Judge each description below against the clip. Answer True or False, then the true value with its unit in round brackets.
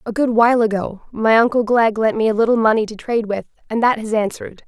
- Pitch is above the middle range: True (225 Hz)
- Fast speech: True (245 wpm)